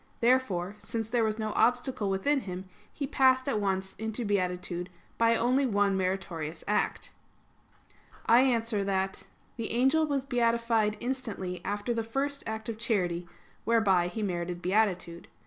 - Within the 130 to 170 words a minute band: Yes, average, 145 wpm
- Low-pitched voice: No, high, 220 Hz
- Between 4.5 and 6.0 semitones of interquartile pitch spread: No, average, 4.0 semitones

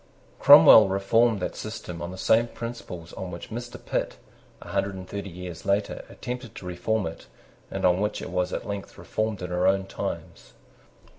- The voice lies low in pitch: Yes, very low, 95 Hz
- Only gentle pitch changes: No, average, 3.3 semitones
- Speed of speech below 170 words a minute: No, average, 180 wpm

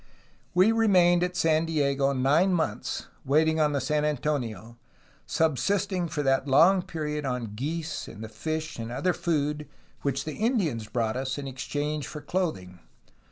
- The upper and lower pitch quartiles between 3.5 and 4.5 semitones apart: Yes, average, 3.9 semitones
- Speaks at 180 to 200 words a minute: No, average, 160 wpm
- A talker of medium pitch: Yes, medium, 150 Hz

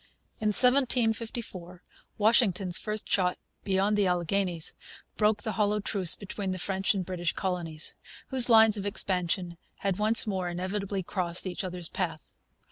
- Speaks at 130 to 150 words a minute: Yes, average, 140 wpm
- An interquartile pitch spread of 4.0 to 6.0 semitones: No, average, 2.8 semitones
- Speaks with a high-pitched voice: Yes, high, 195 Hz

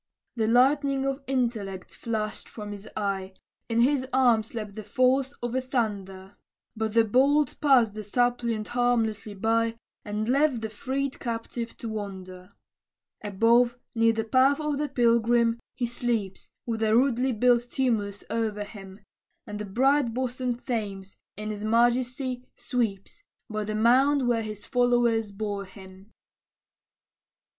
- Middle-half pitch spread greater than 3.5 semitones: No, average, 3.1 semitones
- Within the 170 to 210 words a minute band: No, average, 140 wpm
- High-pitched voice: Yes, high, 230 Hz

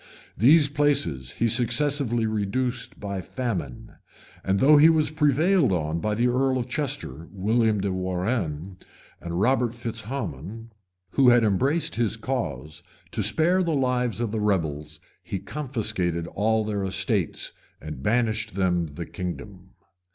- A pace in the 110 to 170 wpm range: Yes, average, 140 wpm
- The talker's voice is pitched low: Yes, low, 110 Hz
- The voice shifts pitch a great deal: Yes, wide, 5.7 semitones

